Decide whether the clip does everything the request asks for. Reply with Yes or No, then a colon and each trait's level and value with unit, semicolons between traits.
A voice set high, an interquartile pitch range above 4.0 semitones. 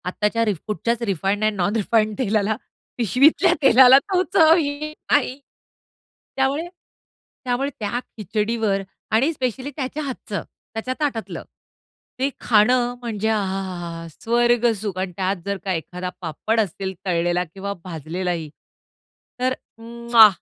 Yes: high, 220 Hz; average, 4.7 semitones